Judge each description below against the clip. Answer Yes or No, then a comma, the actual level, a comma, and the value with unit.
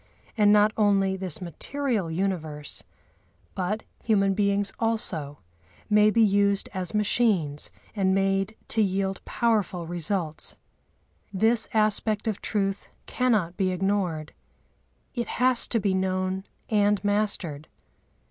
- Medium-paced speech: No, slow, 115 wpm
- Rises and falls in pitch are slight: Yes, narrow, 2.3 semitones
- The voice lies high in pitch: Yes, high, 195 Hz